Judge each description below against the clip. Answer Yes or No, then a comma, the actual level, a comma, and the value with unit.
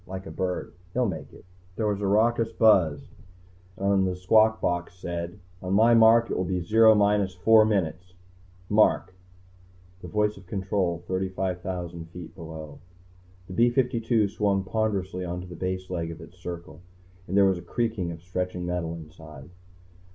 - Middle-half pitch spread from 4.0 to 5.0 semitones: No, average, 3.2 semitones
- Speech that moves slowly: No, average, 165 wpm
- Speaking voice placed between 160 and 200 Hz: No, very low, 95 Hz